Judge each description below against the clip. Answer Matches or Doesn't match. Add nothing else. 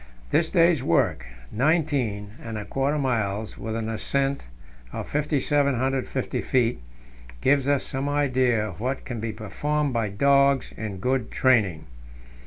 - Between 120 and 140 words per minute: Matches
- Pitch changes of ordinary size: Matches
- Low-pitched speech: Matches